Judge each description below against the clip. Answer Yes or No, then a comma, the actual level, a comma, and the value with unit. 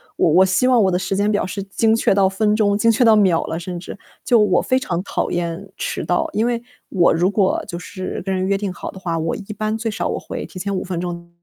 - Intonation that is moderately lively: Yes, average, 3.0 semitones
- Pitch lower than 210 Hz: Yes, high, 195 Hz